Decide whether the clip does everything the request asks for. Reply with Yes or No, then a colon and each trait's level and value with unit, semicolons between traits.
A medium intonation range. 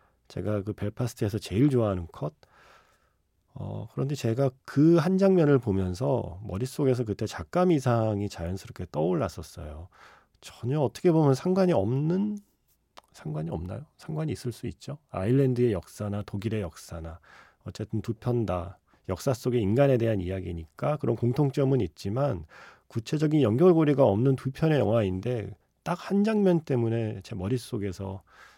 No: wide, 6.0 semitones